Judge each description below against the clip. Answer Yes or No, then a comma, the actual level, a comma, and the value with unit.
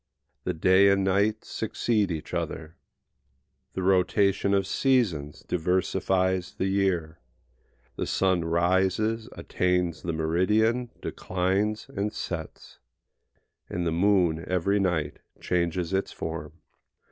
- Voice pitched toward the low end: Yes, very low, 95 Hz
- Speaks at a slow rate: Yes, slow, 110 wpm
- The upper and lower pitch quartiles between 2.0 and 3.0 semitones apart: Yes, narrow, 2.6 semitones